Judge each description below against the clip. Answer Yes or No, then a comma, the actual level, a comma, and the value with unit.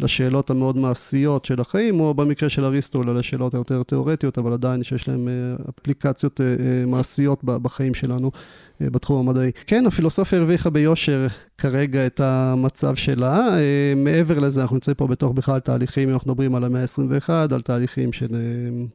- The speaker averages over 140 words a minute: Yes, fast, 150 wpm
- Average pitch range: No, narrow, 2.1 semitones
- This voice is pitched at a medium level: No, low, 130 Hz